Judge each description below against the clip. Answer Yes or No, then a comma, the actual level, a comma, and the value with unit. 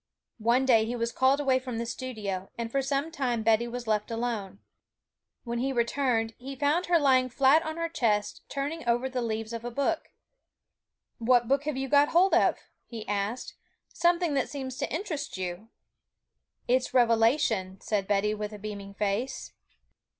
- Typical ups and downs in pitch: Yes, average, 3.8 semitones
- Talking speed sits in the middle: Yes, average, 170 wpm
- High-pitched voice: Yes, high, 245 Hz